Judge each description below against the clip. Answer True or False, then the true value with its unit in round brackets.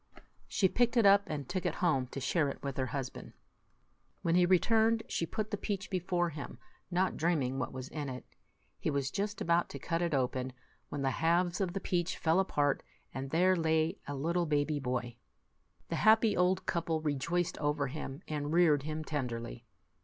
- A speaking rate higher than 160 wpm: True (190 wpm)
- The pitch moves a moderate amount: True (4.5 semitones)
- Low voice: False (160 Hz)